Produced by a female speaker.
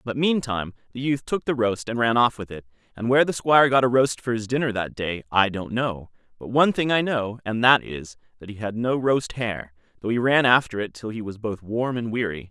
No: male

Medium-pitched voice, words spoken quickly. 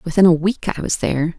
Yes: medium, 175 Hz; fast, 260 wpm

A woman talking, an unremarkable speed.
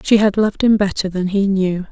No: female; fast, 250 wpm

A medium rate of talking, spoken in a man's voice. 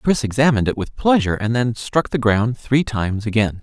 No: fast, 215 wpm; male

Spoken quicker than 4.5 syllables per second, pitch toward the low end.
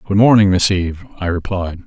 Yes: 5.9 syllables/s; very low, 95 Hz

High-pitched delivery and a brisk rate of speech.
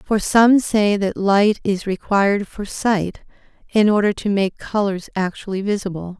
No: high, 200 Hz; average, 155 wpm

